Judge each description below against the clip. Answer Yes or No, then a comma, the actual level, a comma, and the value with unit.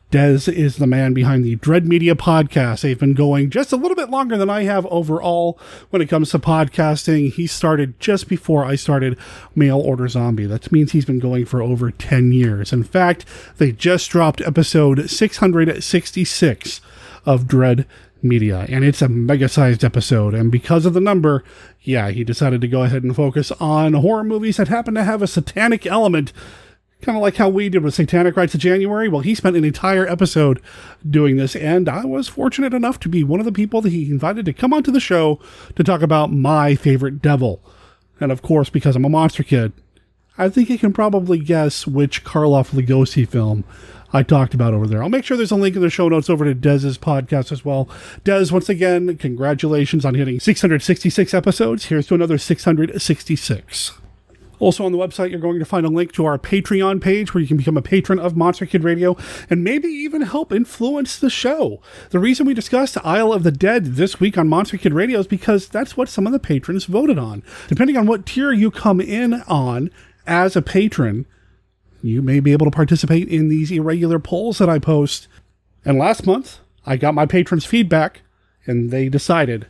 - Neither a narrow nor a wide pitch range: No, wide, 6.0 semitones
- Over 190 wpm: Yes, average, 200 wpm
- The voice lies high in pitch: No, medium, 160 Hz